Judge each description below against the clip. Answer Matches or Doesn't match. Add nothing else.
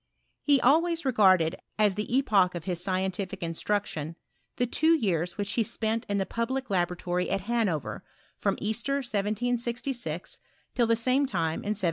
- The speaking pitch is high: Matches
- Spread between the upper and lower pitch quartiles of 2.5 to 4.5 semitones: Doesn't match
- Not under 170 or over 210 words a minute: Doesn't match